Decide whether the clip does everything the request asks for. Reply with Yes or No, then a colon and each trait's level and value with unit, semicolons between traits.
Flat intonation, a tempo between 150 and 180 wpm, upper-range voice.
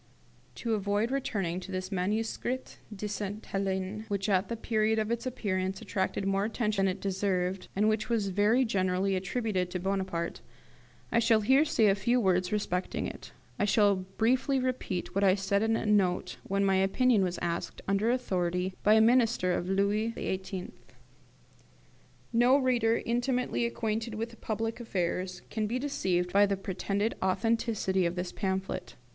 No: average, 3.1 semitones; average, 165 wpm; high, 200 Hz